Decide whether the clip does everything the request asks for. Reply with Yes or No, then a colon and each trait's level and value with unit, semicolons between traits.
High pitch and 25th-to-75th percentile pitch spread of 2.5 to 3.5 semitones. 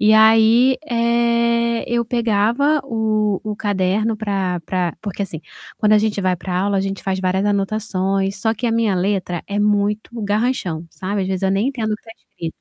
Yes: high, 210 Hz; average, 2.8 semitones